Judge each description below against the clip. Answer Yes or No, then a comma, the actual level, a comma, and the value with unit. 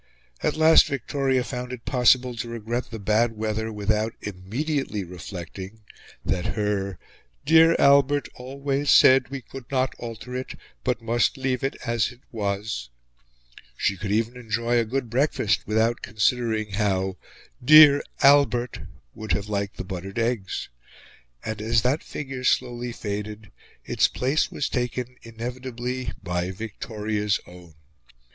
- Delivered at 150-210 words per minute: No, slow, 135 wpm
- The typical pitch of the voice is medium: No, low, 115 Hz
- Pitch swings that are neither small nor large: Yes, average, 3.5 semitones